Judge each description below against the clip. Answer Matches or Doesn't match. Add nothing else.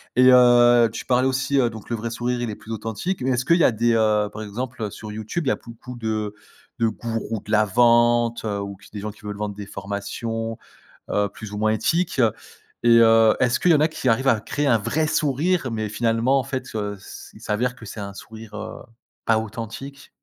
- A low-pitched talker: Matches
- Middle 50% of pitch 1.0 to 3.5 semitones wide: Matches